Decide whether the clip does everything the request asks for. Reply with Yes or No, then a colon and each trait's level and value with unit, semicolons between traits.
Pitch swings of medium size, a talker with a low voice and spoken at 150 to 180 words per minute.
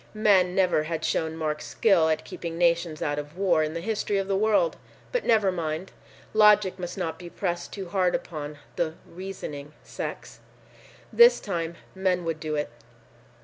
No: average, 3.4 semitones; medium, 175 Hz; average, 170 wpm